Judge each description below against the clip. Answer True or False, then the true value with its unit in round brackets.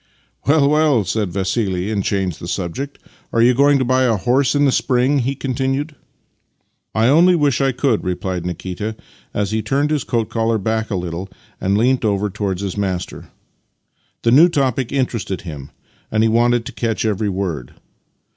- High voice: False (115 Hz)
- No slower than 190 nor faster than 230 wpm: True (195 wpm)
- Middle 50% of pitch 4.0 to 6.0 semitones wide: True (5.4 semitones)